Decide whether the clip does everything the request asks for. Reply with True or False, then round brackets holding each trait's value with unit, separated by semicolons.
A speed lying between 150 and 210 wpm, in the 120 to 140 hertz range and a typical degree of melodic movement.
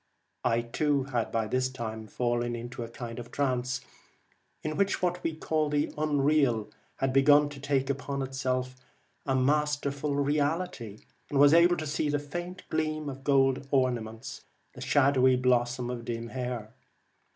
True (155 wpm; 135 Hz; 3.2 semitones)